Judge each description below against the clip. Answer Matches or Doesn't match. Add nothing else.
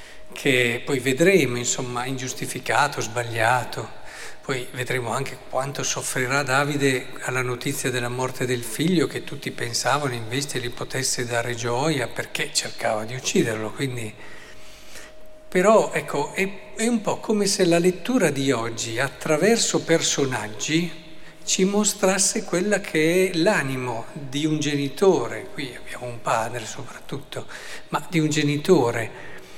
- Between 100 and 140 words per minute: Matches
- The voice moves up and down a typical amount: Matches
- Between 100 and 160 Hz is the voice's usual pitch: Matches